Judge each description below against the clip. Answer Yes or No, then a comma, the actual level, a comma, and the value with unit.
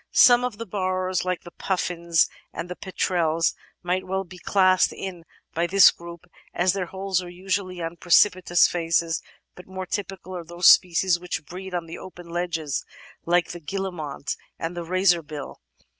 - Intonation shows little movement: Yes, narrow, 1.7 semitones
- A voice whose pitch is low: No, medium, 180 Hz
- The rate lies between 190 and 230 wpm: No, average, 160 wpm